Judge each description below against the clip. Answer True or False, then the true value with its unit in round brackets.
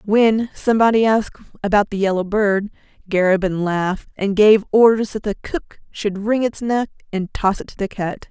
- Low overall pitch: False (205 Hz)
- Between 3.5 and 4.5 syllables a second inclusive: False (4.9 syllables/s)